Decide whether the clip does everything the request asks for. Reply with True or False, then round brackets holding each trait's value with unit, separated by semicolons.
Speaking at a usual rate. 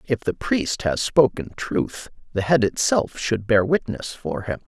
True (175 wpm)